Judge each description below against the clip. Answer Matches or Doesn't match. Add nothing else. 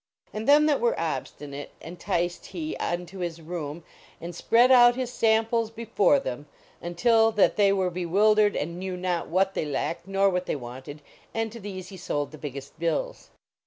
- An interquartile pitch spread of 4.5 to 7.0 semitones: Matches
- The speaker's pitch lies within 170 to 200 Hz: Matches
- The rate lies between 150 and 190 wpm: Matches